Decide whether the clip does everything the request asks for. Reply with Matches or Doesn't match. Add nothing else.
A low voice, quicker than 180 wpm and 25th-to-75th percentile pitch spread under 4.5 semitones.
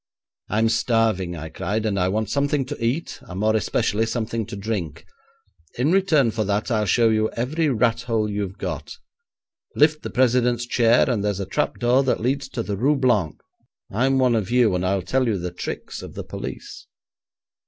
Matches